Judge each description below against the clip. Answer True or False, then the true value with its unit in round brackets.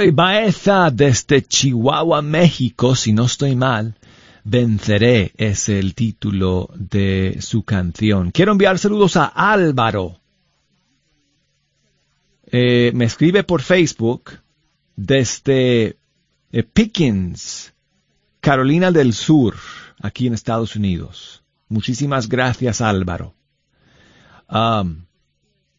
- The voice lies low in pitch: True (120 Hz)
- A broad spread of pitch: True (6.4 semitones)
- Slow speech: True (90 wpm)